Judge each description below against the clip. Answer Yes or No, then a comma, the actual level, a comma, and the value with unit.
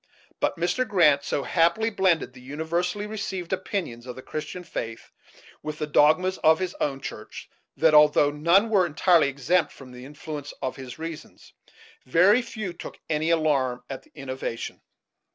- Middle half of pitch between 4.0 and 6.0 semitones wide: Yes, average, 4.6 semitones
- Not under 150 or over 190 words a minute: Yes, average, 160 wpm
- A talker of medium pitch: Yes, medium, 160 Hz